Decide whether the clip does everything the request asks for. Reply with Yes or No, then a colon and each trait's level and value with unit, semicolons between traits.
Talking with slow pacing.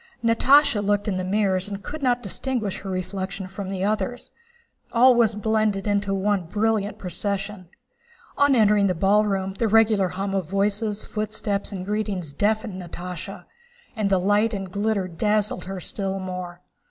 No: average, 155 wpm